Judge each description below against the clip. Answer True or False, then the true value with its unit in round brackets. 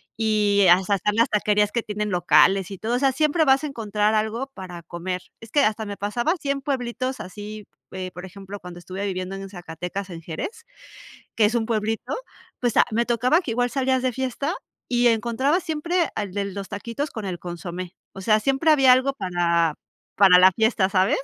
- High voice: True (215 Hz)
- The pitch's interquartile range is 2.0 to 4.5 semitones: False (5.1 semitones)